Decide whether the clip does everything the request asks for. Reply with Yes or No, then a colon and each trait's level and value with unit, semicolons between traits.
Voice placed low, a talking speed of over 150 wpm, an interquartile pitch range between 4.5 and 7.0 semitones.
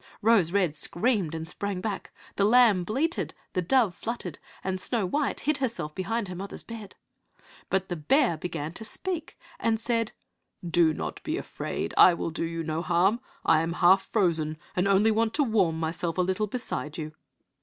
No: high, 190 Hz; average, 180 wpm; average, 5.1 semitones